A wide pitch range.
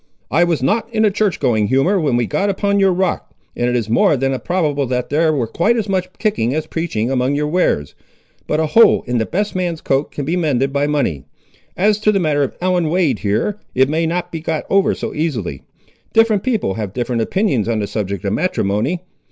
Yes: wide, 7.0 semitones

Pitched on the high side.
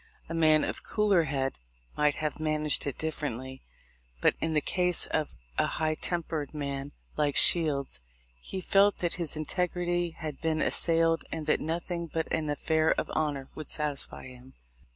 No: medium, 155 Hz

